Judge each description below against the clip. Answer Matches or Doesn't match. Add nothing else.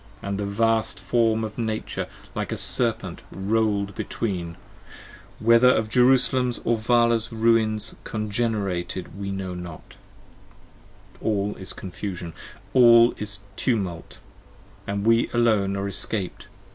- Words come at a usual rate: Doesn't match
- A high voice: Doesn't match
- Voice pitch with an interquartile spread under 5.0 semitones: Matches